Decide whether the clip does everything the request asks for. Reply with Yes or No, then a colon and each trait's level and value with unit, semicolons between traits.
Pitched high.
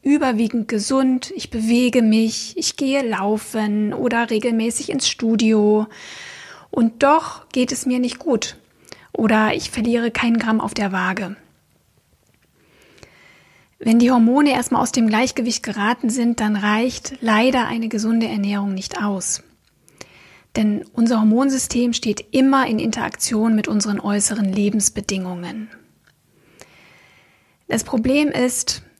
Yes: high, 230 Hz